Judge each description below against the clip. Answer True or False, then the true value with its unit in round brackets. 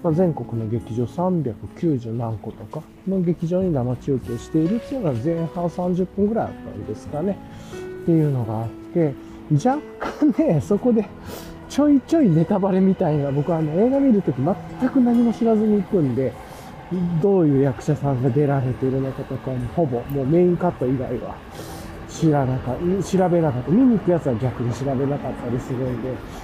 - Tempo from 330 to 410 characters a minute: True (350 characters per minute)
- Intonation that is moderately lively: False (6.5 semitones)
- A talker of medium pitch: True (155 Hz)